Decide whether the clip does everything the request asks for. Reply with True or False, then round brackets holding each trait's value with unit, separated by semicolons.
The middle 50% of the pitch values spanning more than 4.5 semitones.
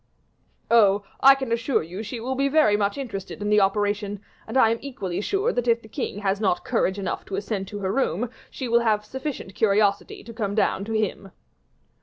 False (2.9 semitones)